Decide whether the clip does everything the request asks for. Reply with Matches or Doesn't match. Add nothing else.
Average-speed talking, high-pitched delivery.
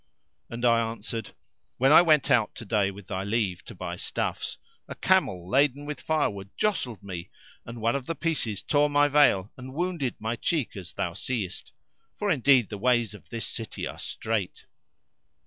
Doesn't match